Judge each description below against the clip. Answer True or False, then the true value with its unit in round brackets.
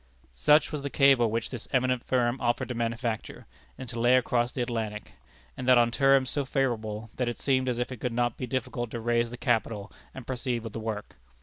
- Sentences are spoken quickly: True (220 wpm)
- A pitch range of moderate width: False (1.9 semitones)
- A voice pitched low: True (120 Hz)